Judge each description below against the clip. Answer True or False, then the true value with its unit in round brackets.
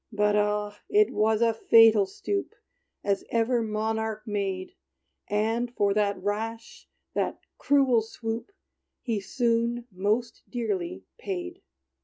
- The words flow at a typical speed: False (115 wpm)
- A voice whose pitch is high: True (220 Hz)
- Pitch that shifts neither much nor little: False (2.1 semitones)